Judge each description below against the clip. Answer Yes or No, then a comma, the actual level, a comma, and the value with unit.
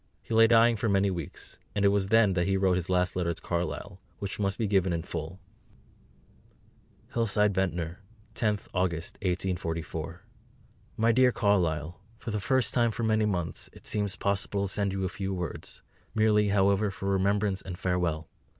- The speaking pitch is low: Yes, very low, 95 Hz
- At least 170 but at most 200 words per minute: Yes, average, 175 wpm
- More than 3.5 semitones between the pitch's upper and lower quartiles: No, average, 2.7 semitones